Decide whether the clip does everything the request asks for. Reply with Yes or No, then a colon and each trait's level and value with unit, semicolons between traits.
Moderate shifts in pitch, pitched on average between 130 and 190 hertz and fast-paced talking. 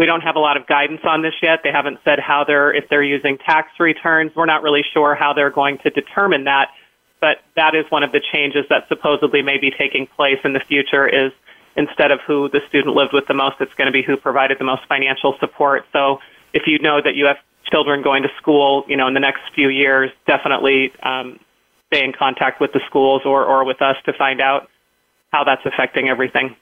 No: narrow, 1.5 semitones; medium, 140 Hz; fast, 230 wpm